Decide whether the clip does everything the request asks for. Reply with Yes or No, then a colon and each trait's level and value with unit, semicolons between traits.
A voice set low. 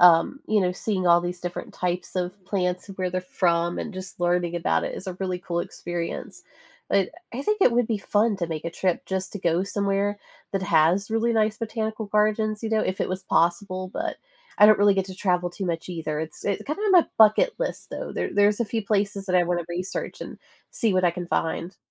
No: medium, 185 Hz